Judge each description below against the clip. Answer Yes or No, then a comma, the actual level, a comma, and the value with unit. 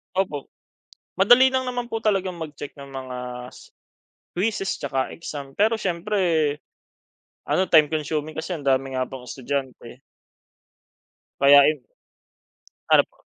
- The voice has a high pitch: No, medium, 155 Hz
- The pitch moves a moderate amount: No, wide, 6.1 semitones